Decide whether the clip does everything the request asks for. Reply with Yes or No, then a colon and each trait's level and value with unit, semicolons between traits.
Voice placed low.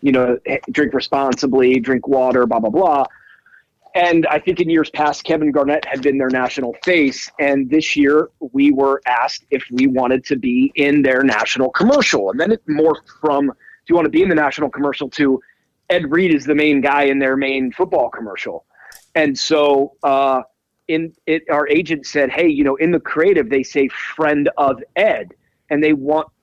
No: medium, 145 Hz